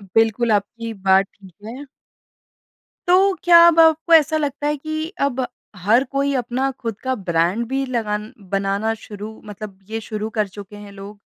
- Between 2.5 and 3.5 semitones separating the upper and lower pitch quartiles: No, wide, 5.4 semitones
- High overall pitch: Yes, high, 225 Hz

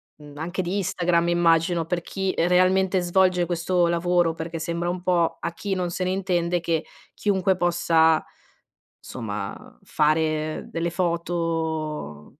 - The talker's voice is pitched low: No, medium, 170 Hz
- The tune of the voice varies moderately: No, narrow, 1.8 semitones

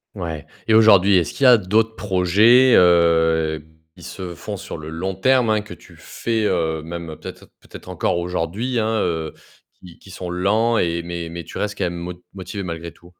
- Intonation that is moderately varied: Yes, average, 4.1 semitones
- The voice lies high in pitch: No, very low, 90 Hz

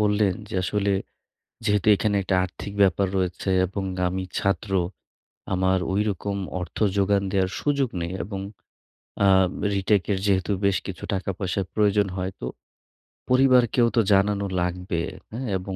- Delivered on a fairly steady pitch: Yes, narrow, 1.7 semitones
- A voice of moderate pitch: No, low, 100 Hz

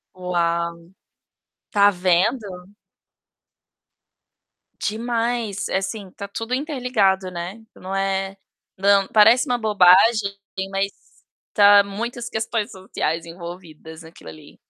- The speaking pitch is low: No, high, 195 Hz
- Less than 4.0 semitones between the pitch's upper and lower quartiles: Yes, average, 3.5 semitones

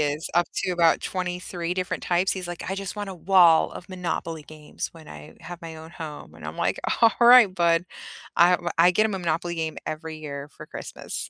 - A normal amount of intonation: No, narrow, 2.3 semitones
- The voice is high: No, medium, 175 Hz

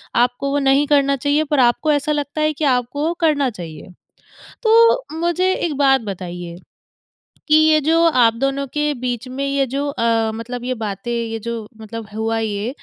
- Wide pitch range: No, average, 4.5 semitones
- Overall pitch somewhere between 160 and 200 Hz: No, very high, 270 Hz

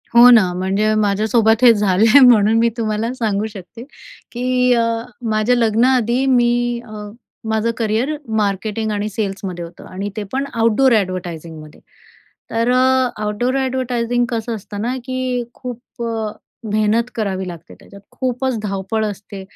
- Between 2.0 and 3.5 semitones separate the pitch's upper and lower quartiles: Yes, average, 3.0 semitones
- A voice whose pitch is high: Yes, high, 220 Hz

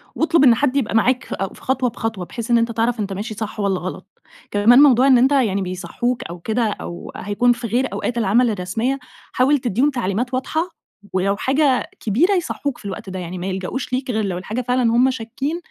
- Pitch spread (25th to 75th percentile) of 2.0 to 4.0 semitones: No, average, 4.5 semitones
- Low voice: No, high, 235 Hz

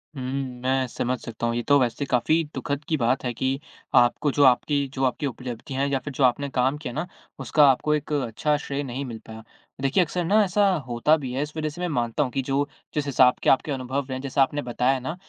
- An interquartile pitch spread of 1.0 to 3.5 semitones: Yes, average, 2.7 semitones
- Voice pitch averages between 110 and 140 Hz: Yes, low, 135 Hz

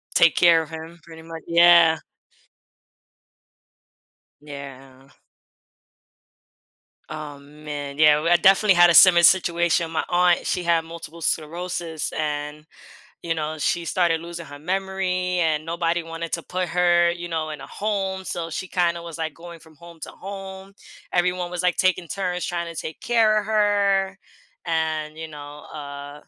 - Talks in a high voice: No, medium, 170 Hz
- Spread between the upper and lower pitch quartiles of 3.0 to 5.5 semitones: No, narrow, 2.4 semitones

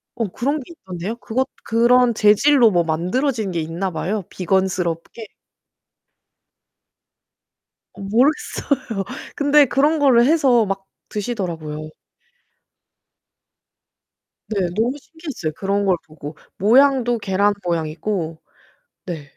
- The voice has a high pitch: Yes, high, 210 Hz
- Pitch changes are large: Yes, wide, 6.1 semitones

